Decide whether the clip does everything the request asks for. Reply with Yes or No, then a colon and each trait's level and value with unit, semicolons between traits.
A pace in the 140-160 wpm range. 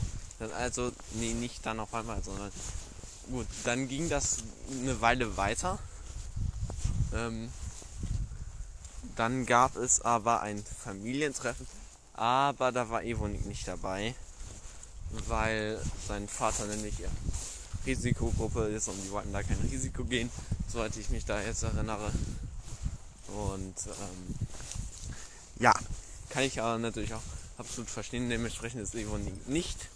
No: slow, 125 wpm